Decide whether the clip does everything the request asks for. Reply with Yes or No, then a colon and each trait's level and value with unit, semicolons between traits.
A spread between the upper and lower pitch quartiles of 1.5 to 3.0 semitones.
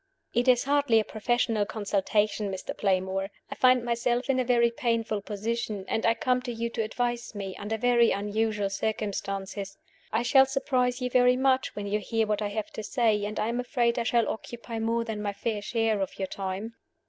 Yes: average, 2.7 semitones